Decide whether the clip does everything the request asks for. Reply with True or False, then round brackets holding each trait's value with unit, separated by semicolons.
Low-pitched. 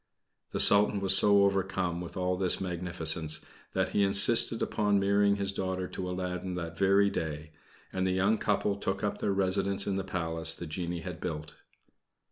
True (95 Hz)